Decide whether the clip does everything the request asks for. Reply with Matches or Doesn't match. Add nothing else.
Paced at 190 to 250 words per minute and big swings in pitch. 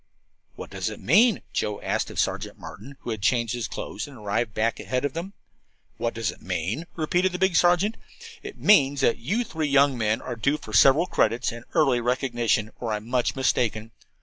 Matches